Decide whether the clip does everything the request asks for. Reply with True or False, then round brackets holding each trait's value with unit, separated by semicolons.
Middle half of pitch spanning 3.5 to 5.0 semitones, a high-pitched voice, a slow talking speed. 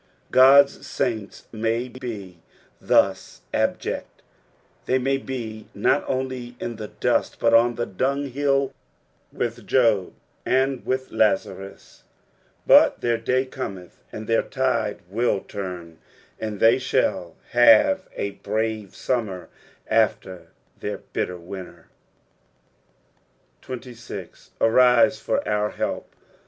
False (3.9 semitones; 115 Hz; 105 wpm)